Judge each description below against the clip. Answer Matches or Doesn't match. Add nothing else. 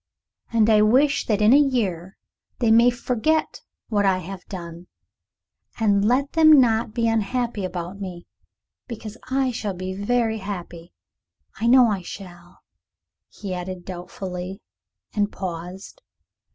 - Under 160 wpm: Matches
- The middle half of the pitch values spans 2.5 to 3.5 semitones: Doesn't match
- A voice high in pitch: Matches